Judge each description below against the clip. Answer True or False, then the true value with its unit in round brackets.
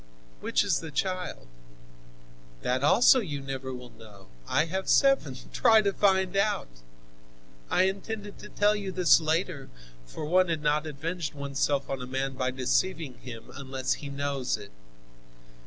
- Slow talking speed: False (155 wpm)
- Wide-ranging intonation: True (6.1 semitones)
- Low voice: False (150 Hz)